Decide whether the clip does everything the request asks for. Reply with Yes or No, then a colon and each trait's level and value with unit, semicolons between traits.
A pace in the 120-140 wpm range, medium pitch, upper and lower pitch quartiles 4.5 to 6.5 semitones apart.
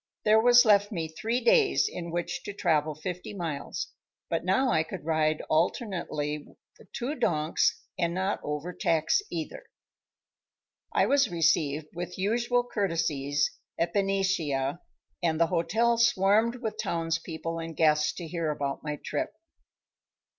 Yes: slow, 135 wpm; medium, 170 Hz; average, 5.2 semitones